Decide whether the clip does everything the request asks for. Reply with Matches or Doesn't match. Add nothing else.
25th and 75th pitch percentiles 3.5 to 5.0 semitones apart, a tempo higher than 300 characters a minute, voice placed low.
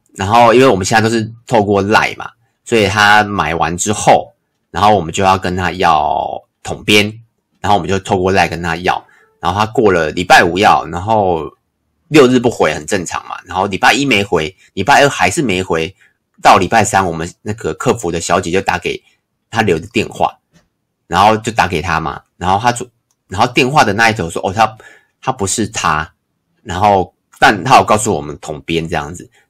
Doesn't match